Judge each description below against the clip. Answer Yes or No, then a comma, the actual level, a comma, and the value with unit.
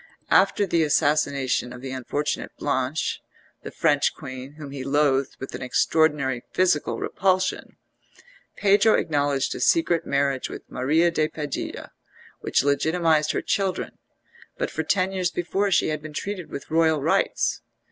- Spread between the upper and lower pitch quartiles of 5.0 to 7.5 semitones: No, average, 3.7 semitones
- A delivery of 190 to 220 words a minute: No, average, 145 wpm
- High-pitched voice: No, medium, 150 Hz